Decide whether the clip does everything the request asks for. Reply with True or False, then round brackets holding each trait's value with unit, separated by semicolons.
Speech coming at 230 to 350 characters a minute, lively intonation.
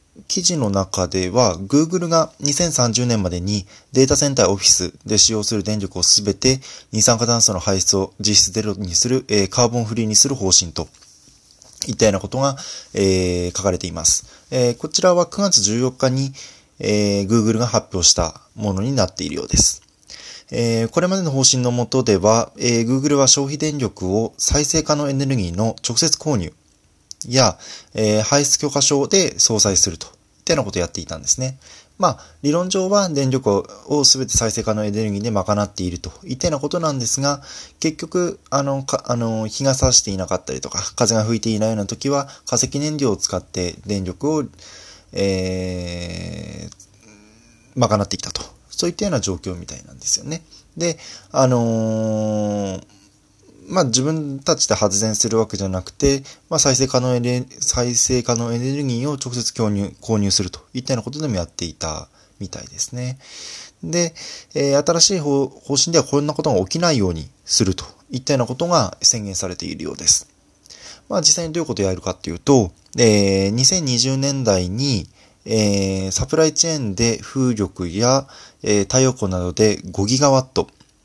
True (335 characters per minute; 5.7 semitones)